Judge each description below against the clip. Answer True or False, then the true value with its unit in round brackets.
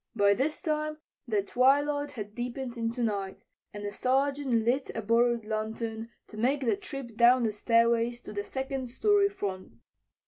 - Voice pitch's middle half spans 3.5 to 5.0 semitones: True (3.9 semitones)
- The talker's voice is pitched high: True (240 Hz)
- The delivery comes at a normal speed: True (165 wpm)